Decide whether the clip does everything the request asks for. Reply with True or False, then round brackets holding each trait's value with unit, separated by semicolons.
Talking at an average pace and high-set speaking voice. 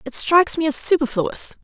True (185 wpm; 290 Hz)